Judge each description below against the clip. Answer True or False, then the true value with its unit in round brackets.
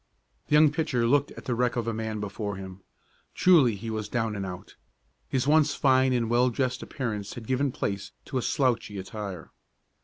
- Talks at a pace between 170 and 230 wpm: True (190 wpm)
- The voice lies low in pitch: True (120 Hz)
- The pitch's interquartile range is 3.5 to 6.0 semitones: True (4.0 semitones)